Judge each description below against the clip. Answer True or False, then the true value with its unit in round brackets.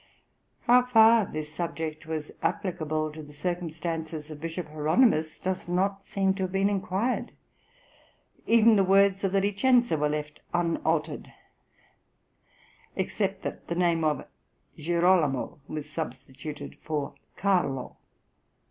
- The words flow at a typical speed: False (120 wpm)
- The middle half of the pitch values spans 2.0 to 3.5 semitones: False (4.2 semitones)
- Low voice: False (170 Hz)